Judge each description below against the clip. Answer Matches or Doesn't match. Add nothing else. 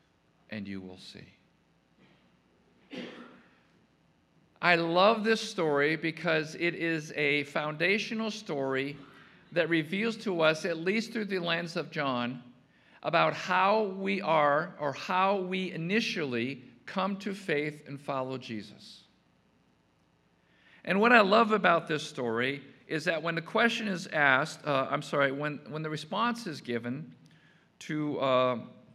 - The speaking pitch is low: Doesn't match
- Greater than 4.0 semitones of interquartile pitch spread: Matches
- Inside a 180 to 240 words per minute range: Doesn't match